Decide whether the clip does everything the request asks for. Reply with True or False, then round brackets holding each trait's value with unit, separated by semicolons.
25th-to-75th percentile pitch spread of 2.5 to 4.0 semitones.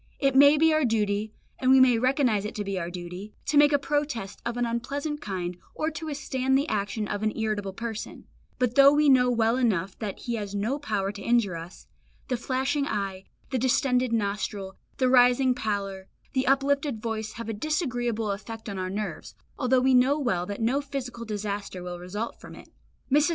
False (4.6 semitones)